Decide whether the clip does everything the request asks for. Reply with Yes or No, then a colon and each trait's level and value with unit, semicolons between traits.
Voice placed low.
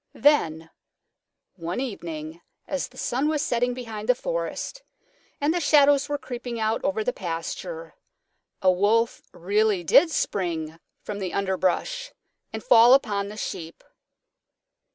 No: high, 220 Hz